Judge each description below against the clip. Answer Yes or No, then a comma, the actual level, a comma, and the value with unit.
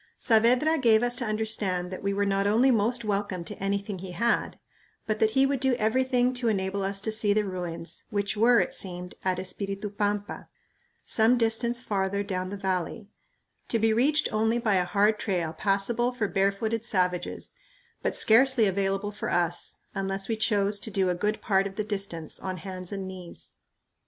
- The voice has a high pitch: Yes, high, 205 Hz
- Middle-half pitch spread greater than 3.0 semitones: No, average, 2.7 semitones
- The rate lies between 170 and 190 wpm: Yes, average, 185 wpm